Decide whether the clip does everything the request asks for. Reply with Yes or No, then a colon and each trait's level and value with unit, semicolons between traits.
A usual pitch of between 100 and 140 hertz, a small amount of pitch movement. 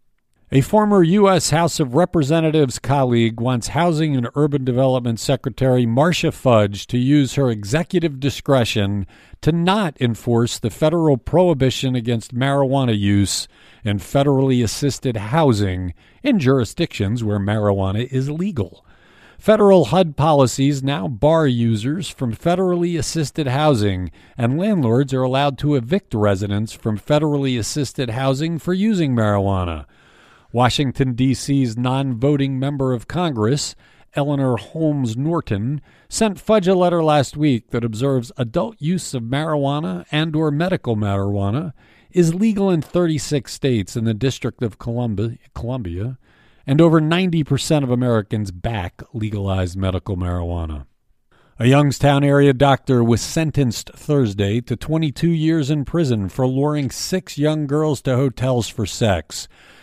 No: low, 135 Hz; average, 5.1 semitones